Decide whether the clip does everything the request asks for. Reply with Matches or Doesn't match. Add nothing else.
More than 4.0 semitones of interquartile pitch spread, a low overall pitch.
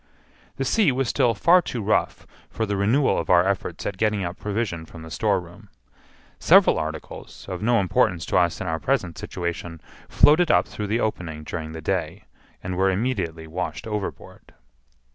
Matches